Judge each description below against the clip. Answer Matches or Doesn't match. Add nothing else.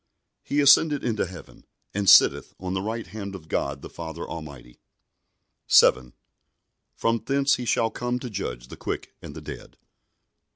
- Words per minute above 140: Matches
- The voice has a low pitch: Matches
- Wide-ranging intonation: Matches